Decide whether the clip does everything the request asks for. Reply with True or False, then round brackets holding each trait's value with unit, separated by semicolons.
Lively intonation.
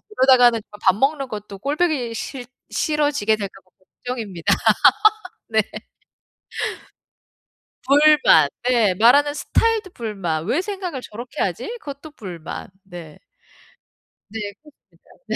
True (6.2 semitones)